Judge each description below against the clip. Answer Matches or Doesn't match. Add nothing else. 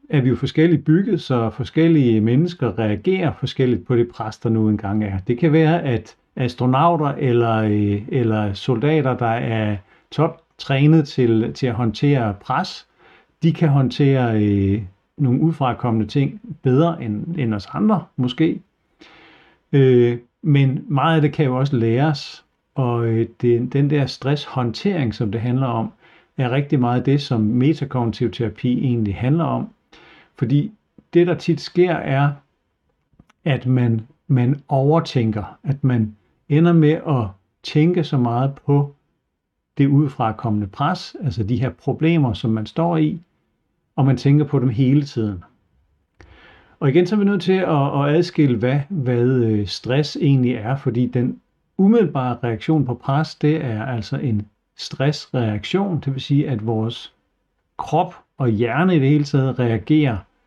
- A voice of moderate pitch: Doesn't match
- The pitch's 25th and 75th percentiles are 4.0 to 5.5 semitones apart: Matches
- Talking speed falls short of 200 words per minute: Matches